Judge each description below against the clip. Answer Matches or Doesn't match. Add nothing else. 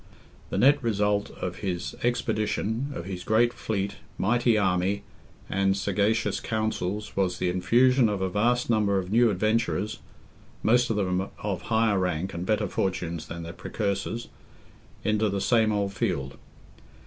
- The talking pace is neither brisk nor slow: Matches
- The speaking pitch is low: Matches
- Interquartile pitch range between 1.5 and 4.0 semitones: Matches